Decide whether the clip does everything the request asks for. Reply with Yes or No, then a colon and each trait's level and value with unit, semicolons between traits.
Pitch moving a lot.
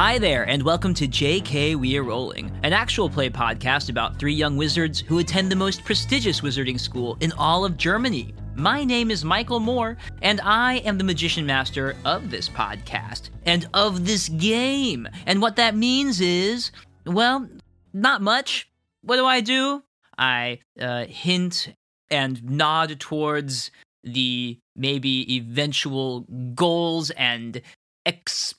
Yes: wide, 7.3 semitones